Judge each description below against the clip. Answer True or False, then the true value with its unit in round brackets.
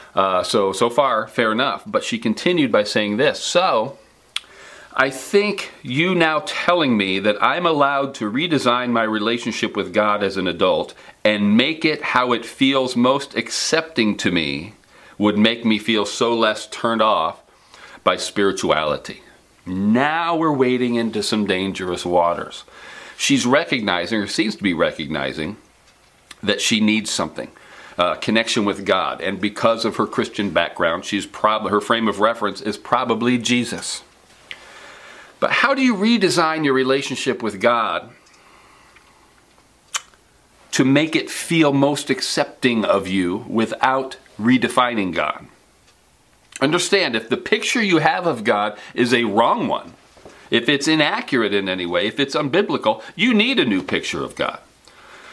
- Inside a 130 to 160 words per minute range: True (145 wpm)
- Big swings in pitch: True (6.4 semitones)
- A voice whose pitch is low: True (120 Hz)